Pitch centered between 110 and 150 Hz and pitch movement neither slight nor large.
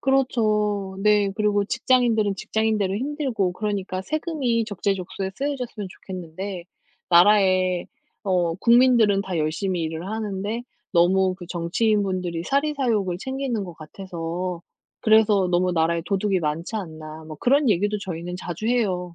No: high, 195 Hz; average, 3.7 semitones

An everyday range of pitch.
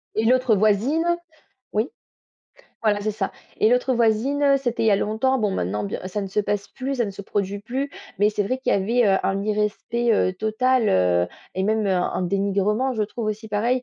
Yes: average, 3.6 semitones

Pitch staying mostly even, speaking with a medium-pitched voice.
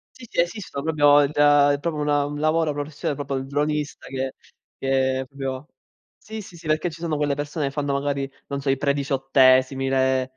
Yes: narrow, 1.9 semitones; medium, 145 Hz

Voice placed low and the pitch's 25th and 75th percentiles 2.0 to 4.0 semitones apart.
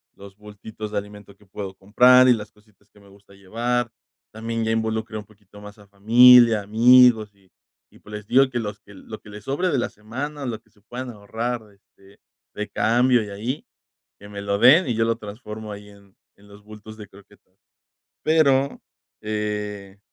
Yes: low, 105 Hz; average, 2.7 semitones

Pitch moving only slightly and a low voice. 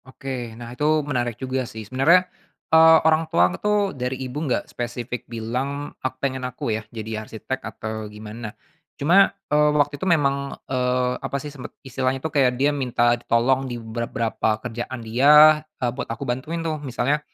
No: average, 3.5 semitones; low, 130 Hz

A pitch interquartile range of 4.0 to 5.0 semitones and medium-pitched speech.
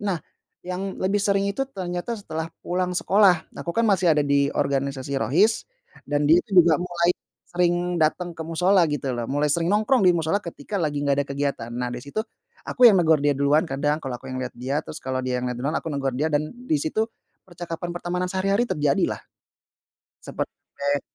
Yes: average, 4.7 semitones; medium, 160 Hz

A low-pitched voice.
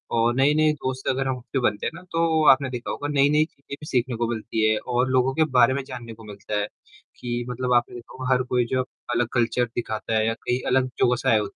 Yes: low, 125 Hz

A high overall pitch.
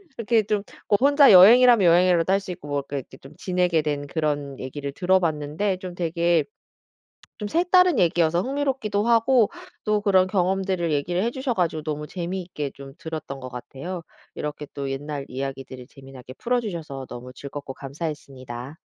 No: medium, 170 Hz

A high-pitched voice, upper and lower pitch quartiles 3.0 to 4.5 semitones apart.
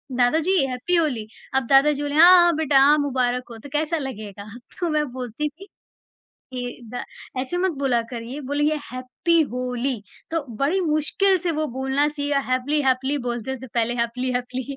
Yes: very high, 270 Hz; average, 3.4 semitones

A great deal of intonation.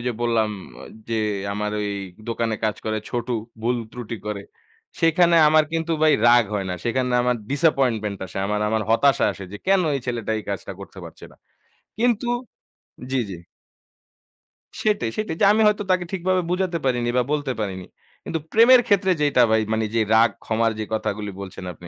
Yes: wide, 7.3 semitones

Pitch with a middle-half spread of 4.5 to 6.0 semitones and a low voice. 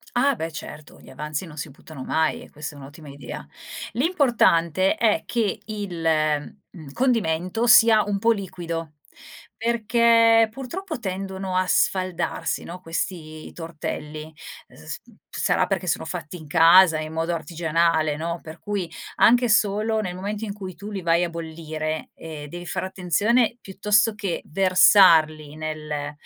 No: average, 5.0 semitones; medium, 175 Hz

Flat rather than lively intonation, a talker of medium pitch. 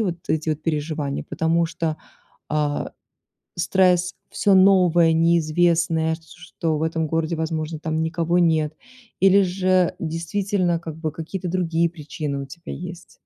Yes: narrow, 1.9 semitones; medium, 165 Hz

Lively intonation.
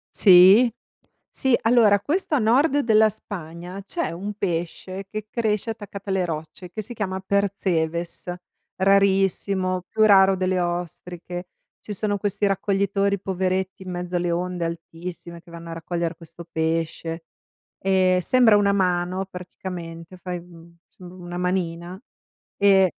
No: narrow, 2.5 semitones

